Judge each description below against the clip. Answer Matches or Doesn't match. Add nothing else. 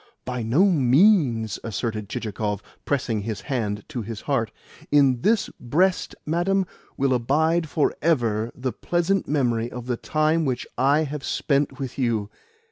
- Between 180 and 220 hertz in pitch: Doesn't match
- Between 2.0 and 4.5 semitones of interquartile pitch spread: Doesn't match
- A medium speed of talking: Matches